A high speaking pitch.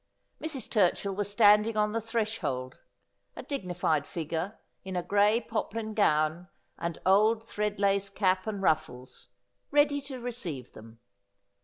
Yes: high, 200 Hz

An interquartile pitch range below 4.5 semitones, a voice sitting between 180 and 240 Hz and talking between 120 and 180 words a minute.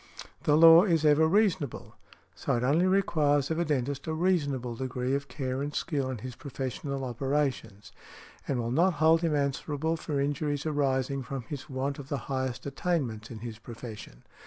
No: average, 3.4 semitones; medium, 140 Hz; average, 175 wpm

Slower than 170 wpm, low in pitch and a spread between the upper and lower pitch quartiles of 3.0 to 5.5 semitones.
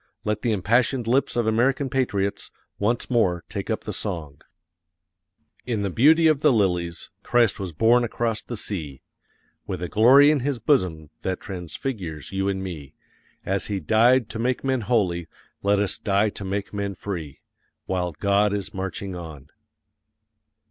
Yes: average, 160 wpm; low, 100 Hz; average, 4.7 semitones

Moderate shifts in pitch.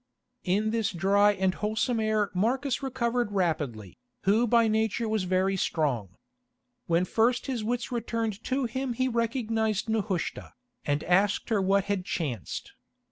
Yes: average, 3.7 semitones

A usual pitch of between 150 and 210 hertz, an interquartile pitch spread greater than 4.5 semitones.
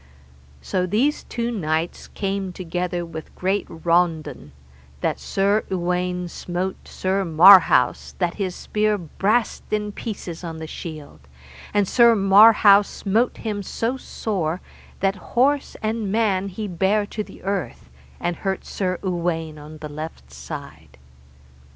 No: medium, 185 Hz; average, 3.7 semitones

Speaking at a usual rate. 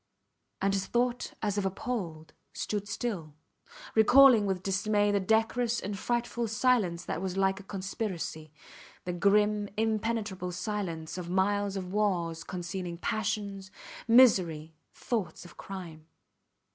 No: slow, 125 wpm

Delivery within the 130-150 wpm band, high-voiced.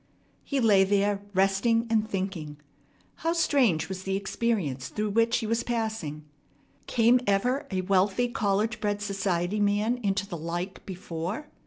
Yes: average, 145 wpm; high, 205 Hz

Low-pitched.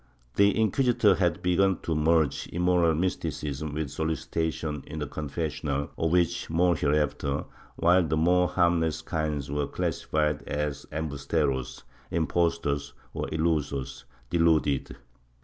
Yes: very low, 80 Hz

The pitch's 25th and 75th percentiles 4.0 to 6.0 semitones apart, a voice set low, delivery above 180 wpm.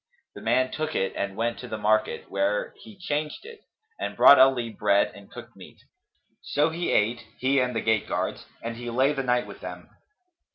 Yes: average, 4.6 semitones; low, 125 Hz; average, 200 wpm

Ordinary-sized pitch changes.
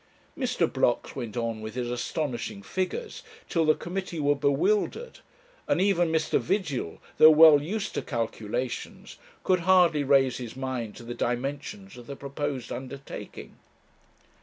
No: wide, 5.9 semitones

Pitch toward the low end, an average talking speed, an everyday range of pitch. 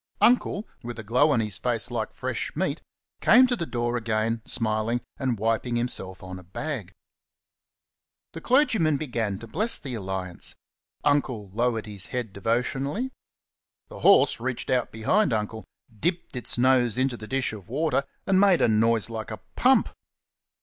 Yes: low, 120 Hz; average, 160 wpm; average, 4.3 semitones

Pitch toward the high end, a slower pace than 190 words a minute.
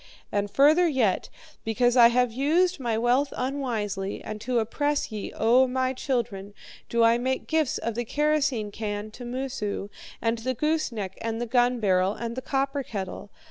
Yes: high, 240 Hz; average, 170 wpm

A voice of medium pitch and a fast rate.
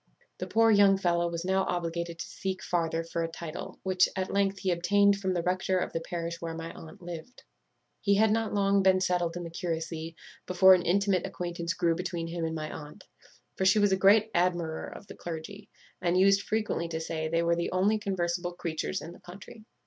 Yes: medium, 175 Hz; fast, 210 wpm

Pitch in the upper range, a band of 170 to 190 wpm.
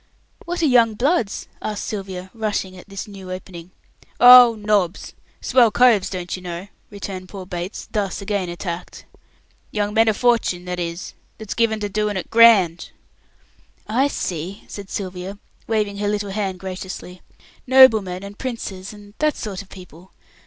No: high, 200 Hz; average, 155 wpm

